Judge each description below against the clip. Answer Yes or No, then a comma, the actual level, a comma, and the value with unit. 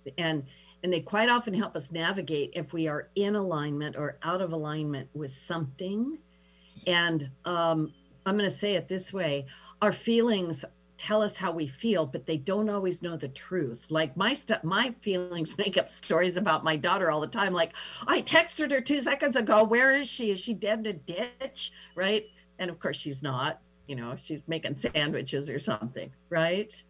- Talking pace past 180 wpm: Yes, average, 190 wpm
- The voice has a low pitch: No, medium, 175 Hz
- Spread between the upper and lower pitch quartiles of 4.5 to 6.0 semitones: Yes, average, 5.2 semitones